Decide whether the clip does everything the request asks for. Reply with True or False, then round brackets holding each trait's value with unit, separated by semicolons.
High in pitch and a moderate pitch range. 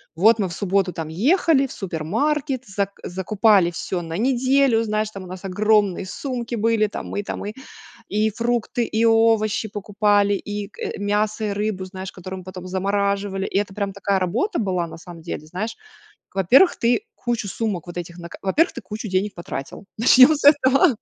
True (205 Hz; 3.4 semitones)